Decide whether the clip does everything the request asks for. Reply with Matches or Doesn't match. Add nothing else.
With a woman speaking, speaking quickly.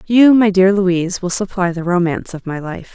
Matches